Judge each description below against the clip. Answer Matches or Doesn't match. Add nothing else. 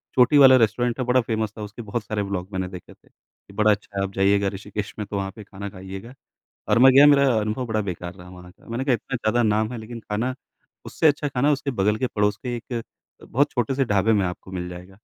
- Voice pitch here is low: Matches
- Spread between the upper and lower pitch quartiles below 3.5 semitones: Doesn't match